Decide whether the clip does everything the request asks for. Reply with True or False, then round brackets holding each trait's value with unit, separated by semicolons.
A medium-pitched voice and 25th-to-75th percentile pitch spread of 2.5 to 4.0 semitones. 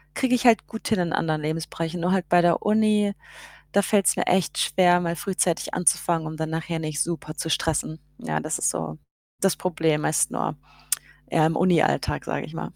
True (170 Hz; 2.9 semitones)